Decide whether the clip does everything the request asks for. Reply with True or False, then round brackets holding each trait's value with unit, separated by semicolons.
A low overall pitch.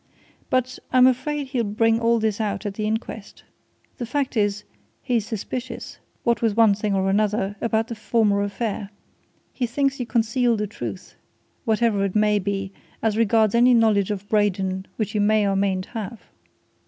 False (215 Hz)